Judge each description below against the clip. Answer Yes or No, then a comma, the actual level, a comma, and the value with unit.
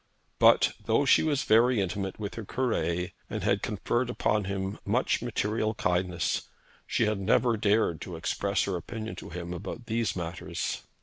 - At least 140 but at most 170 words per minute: Yes, average, 165 wpm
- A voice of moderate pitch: No, low, 100 Hz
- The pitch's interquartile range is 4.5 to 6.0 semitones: No, average, 4.0 semitones